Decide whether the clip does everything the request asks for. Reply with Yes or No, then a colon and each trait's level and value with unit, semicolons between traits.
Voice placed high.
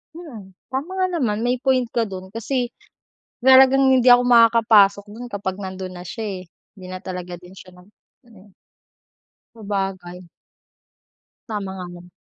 Yes: high, 210 Hz